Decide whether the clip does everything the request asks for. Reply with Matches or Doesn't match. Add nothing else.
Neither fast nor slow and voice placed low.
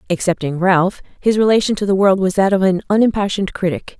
Doesn't match